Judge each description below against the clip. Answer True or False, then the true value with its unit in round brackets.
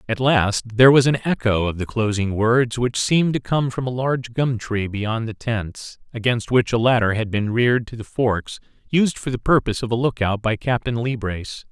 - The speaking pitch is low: True (120 Hz)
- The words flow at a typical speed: False (220 wpm)